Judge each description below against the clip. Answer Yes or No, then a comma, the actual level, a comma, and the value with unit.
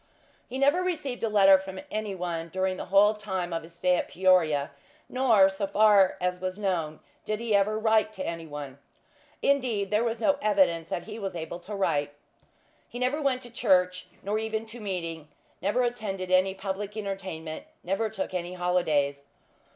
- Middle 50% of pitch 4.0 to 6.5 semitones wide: No, average, 3.5 semitones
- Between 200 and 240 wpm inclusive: No, average, 180 wpm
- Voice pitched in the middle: No, high, 195 Hz